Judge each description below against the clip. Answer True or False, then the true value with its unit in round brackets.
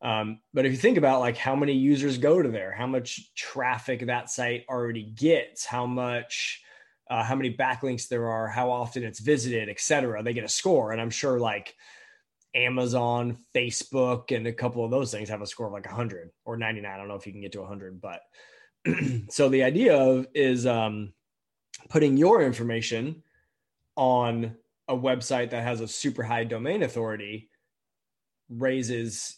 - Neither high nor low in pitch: False (120 Hz)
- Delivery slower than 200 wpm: True (180 wpm)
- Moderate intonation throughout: False (2.3 semitones)